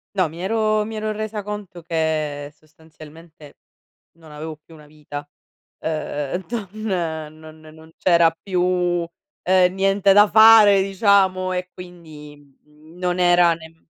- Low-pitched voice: No, medium, 175 Hz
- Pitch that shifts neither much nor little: Yes, average, 3.7 semitones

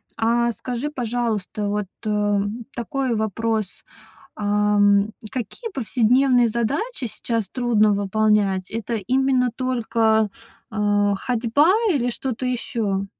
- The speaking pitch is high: Yes, high, 225 Hz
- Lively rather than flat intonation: No, average, 3.1 semitones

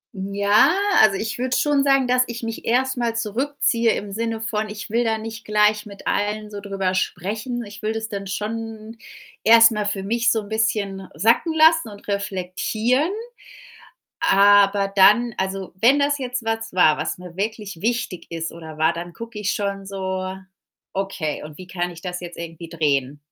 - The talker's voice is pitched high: Yes, high, 210 Hz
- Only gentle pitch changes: No, average, 3.3 semitones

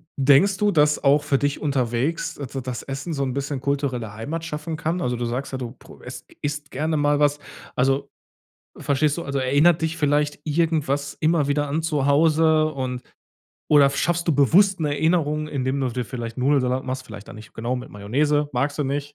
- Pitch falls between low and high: Yes, medium, 145 Hz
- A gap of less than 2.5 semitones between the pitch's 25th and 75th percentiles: No, average, 2.8 semitones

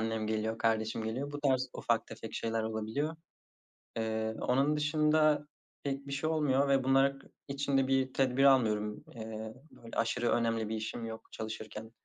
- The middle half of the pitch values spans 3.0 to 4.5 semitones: Yes, average, 3.8 semitones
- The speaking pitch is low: Yes, low, 125 Hz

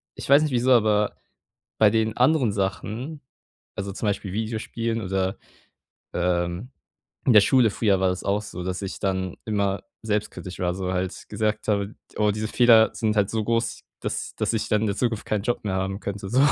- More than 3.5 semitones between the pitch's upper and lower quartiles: No, average, 2.8 semitones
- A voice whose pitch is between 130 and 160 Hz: No, low, 105 Hz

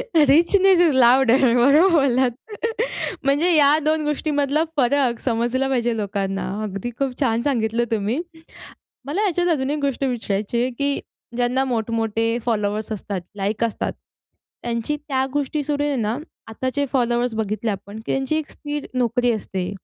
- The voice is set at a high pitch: Yes, very high, 250 Hz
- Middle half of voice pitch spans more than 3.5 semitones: Yes, average, 4.2 semitones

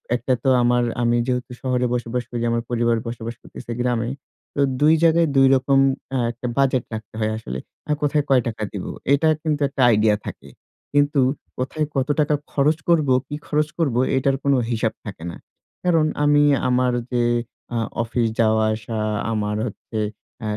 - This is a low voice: Yes, low, 125 Hz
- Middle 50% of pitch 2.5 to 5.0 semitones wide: Yes, average, 3.7 semitones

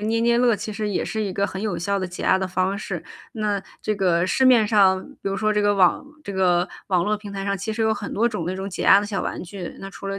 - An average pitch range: No, narrow, 2.1 semitones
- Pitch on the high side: Yes, high, 200 Hz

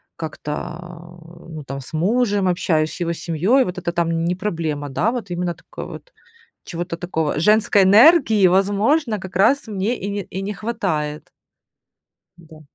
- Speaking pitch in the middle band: Yes, medium, 180 Hz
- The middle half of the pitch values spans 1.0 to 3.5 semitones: No, average, 4.0 semitones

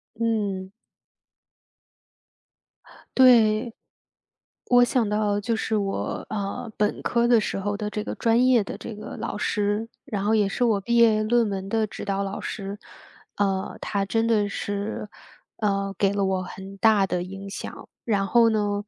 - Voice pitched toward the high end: Yes, high, 210 Hz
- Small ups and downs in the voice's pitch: Yes, narrow, 2.3 semitones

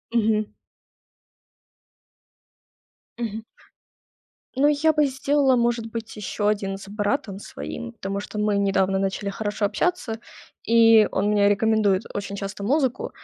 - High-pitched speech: Yes, high, 210 Hz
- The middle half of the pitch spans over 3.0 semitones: No, narrow, 2.6 semitones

